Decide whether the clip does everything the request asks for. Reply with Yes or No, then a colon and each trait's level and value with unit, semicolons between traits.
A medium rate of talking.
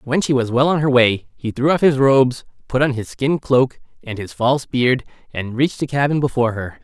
No: fast, 235 wpm